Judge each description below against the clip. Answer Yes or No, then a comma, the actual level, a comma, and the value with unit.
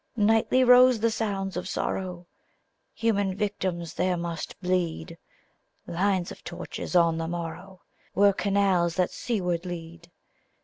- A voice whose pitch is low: No, medium, 185 Hz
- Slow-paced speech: Yes, slow, 125 wpm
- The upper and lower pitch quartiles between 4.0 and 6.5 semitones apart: No, average, 2.8 semitones